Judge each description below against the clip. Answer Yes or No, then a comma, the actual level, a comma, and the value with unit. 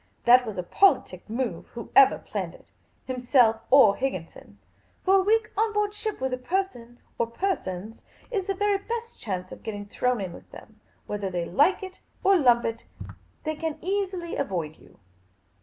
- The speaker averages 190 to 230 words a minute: No, average, 180 wpm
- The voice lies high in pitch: Yes, very high, 255 Hz